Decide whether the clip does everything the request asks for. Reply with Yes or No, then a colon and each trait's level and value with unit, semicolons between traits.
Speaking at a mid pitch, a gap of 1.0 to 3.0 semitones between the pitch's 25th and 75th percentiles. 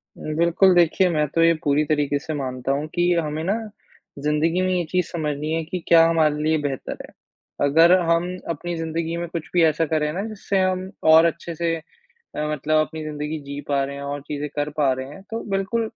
Yes: medium, 160 Hz; narrow, 2.5 semitones